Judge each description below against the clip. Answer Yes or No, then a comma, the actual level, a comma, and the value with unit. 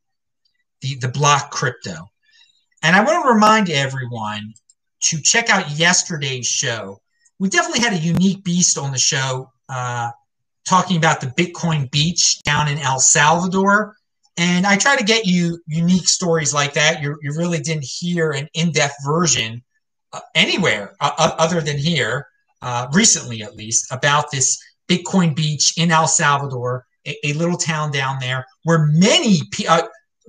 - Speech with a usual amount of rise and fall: Yes, average, 4.7 semitones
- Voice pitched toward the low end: No, medium, 160 Hz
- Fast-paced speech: No, average, 160 wpm